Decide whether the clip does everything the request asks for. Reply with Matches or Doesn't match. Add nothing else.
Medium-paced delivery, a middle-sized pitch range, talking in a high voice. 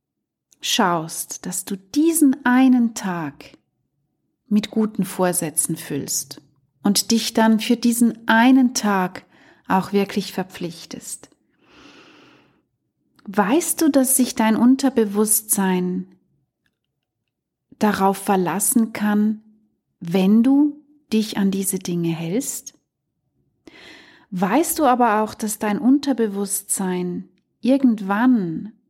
Doesn't match